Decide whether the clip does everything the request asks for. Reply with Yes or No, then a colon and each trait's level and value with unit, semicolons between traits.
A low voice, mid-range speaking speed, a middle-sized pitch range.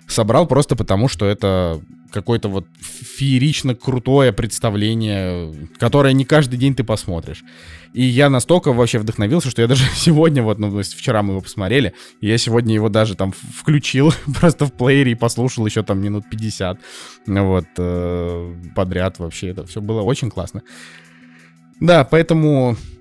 No: low, 110 Hz; average, 150 wpm; wide, 6.0 semitones